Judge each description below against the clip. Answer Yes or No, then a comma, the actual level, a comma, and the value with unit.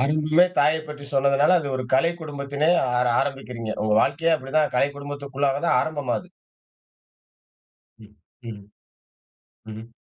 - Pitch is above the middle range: No, medium, 140 Hz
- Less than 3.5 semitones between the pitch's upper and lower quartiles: Yes, narrow, 2.6 semitones